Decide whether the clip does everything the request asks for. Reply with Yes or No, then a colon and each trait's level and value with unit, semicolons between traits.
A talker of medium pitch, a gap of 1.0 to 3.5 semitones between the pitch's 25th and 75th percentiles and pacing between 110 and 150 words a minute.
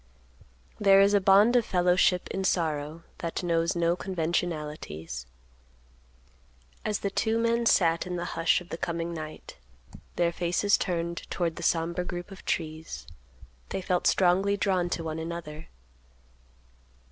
Yes: medium, 175 Hz; narrow, 2.6 semitones; average, 140 wpm